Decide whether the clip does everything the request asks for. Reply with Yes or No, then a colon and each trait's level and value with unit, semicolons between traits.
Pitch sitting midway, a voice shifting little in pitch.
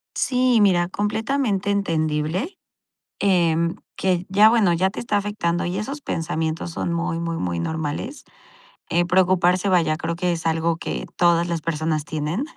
No: medium, 175 Hz; average, 3.6 semitones